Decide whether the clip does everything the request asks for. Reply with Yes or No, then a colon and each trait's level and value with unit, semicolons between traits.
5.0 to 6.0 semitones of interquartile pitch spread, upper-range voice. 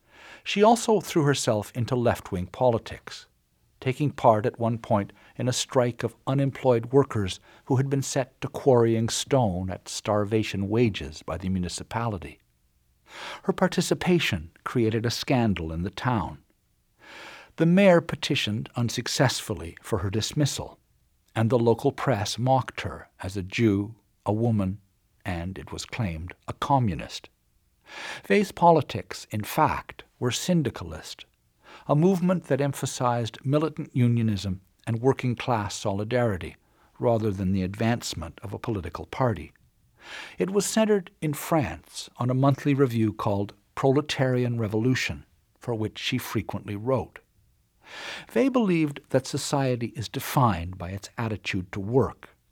No: average, 5.3 semitones; low, 115 Hz